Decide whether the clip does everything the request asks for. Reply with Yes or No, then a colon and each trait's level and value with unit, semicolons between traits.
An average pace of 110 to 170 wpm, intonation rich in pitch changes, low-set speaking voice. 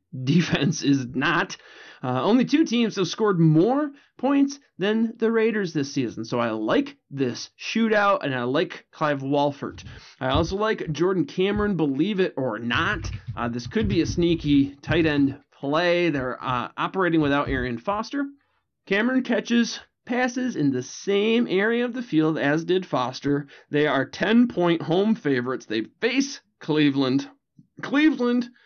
No: average, 155 wpm; wide, 8.3 semitones; medium, 170 Hz